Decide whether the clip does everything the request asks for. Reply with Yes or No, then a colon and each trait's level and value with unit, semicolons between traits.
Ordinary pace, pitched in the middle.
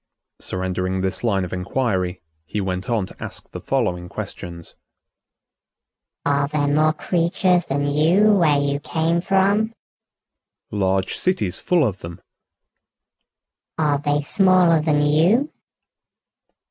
No: slow, 120 wpm; medium, 145 Hz